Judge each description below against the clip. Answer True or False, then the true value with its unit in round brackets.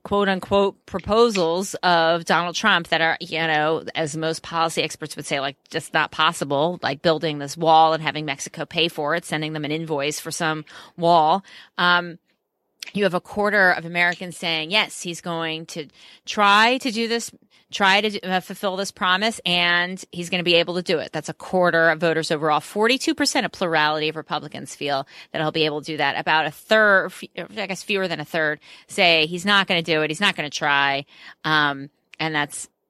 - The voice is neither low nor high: True (170 Hz)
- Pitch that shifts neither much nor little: True (3.4 semitones)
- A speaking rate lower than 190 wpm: False (205 wpm)